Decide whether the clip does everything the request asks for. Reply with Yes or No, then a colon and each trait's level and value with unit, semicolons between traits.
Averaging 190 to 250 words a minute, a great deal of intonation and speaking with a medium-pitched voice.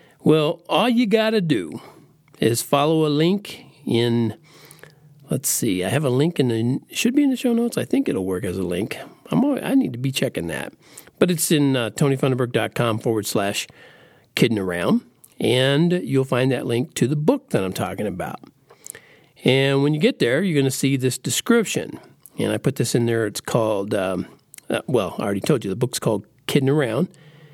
Yes: average, 200 wpm; wide, 5.9 semitones; medium, 145 Hz